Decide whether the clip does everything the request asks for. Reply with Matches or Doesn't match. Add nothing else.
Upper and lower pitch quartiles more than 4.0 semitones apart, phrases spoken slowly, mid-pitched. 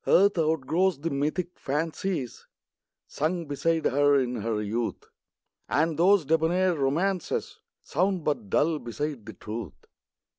Matches